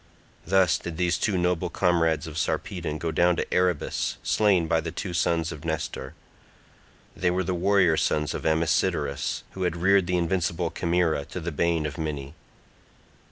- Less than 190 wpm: Yes, average, 165 wpm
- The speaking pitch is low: Yes, very low, 85 Hz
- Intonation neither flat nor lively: No, narrow, 2.1 semitones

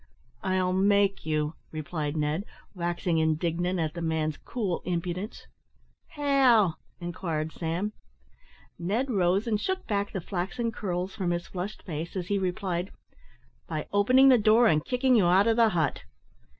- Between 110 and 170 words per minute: Yes, average, 150 wpm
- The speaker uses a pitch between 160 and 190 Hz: Yes, medium, 185 Hz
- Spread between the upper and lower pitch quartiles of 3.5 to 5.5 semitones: Yes, average, 4.0 semitones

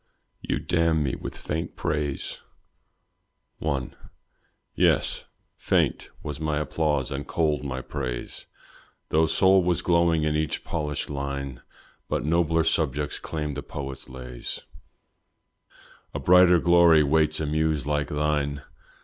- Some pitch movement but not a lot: No, narrow, 2.3 semitones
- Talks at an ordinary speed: No, slow, 125 wpm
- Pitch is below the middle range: Yes, very low, 75 Hz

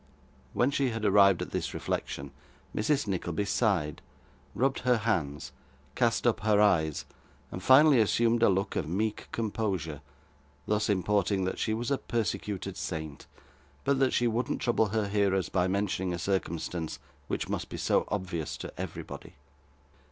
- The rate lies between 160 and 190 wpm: No, average, 150 wpm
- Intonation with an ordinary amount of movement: Yes, average, 3.9 semitones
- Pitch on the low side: Yes, low, 100 Hz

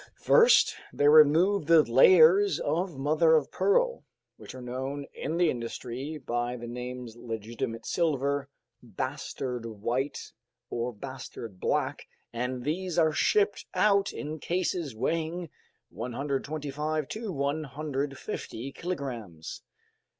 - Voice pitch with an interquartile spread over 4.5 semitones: Yes, average, 4.9 semitones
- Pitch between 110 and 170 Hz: Yes, medium, 140 Hz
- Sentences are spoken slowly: Yes, slow, 110 wpm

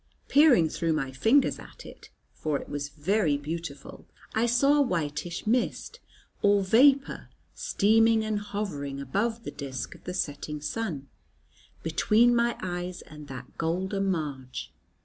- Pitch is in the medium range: Yes, medium, 180 Hz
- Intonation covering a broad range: Yes, wide, 7.3 semitones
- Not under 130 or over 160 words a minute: Yes, average, 140 wpm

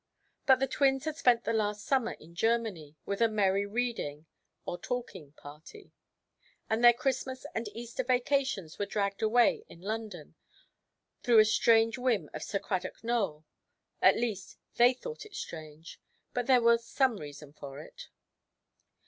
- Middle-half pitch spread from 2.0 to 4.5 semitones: No, average, 5.3 semitones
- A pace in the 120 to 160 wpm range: Yes, average, 155 wpm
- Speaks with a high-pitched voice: Yes, high, 225 Hz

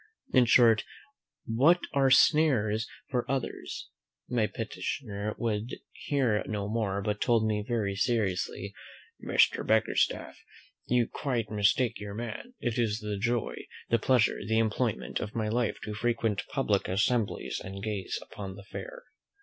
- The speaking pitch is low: Yes, low, 110 Hz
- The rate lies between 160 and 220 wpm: No, average, 140 wpm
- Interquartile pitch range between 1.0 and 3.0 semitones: Yes, average, 2.7 semitones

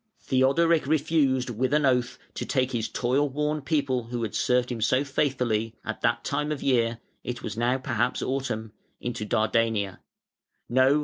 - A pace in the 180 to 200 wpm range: No, average, 170 wpm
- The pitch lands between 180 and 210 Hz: No, low, 125 Hz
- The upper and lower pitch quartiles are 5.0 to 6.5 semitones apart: No, average, 3.0 semitones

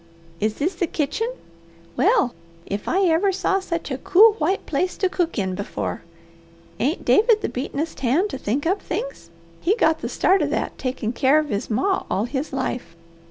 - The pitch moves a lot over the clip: Yes, wide, 6.8 semitones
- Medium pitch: No, very high, 320 Hz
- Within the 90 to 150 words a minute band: No, average, 185 wpm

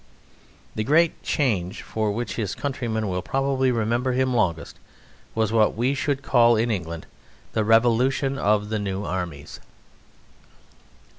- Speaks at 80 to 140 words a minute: Yes, slow, 135 wpm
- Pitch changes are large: No, average, 4.1 semitones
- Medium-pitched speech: No, low, 115 Hz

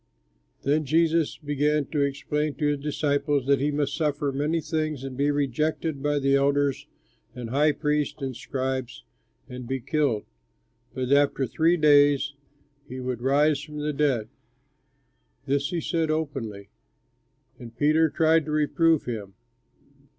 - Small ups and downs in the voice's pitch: Yes, narrow, 2.2 semitones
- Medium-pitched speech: Yes, medium, 145 Hz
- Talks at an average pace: Yes, average, 145 wpm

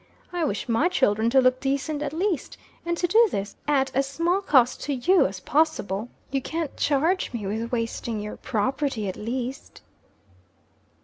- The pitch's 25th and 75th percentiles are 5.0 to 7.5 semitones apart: Yes, wide, 5.6 semitones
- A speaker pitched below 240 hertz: No, very high, 270 Hz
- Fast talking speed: No, average, 170 wpm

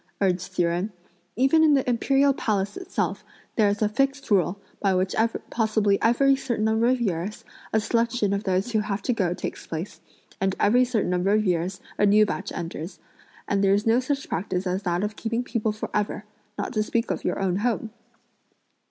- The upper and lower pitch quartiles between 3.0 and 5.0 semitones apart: Yes, average, 3.6 semitones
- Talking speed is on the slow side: No, average, 190 wpm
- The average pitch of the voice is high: Yes, high, 210 Hz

